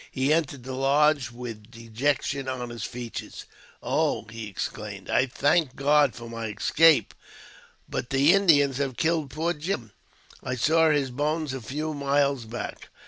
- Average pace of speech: Yes, average, 150 wpm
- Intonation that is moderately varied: Yes, average, 3.6 semitones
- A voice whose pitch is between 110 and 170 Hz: Yes, low, 135 Hz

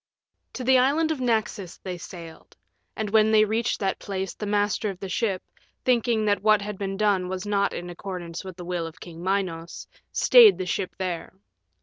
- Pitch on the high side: Yes, high, 200 Hz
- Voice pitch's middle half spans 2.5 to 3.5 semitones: Yes, average, 3.1 semitones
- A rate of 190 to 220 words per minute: Yes, average, 200 wpm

